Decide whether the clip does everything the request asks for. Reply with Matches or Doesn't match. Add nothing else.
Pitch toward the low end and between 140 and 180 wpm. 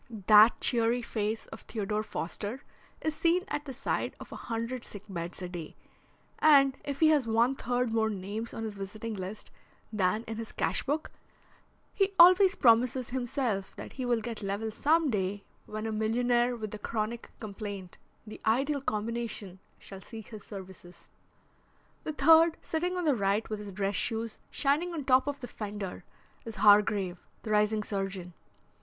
Doesn't match